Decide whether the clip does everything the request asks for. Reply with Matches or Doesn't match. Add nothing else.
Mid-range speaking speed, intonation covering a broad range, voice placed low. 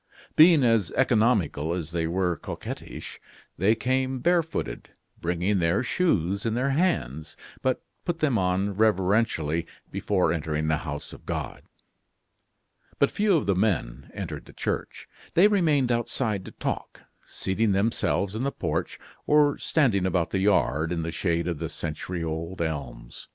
Matches